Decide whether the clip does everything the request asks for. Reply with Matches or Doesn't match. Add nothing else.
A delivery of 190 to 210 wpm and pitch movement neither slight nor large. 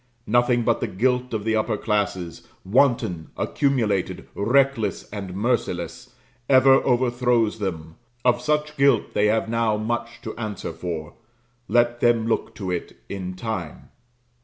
Doesn't match